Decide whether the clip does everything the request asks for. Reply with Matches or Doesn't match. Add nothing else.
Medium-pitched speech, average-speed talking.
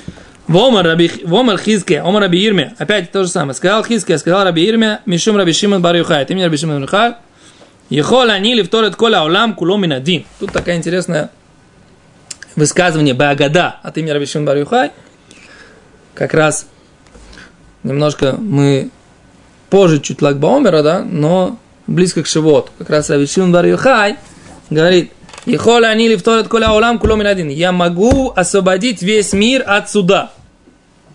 Matches